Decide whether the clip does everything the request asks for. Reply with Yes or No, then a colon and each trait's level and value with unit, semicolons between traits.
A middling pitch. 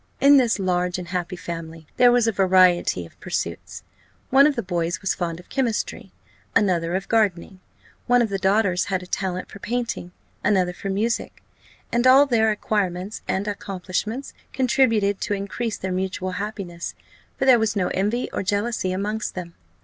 No: high, 195 Hz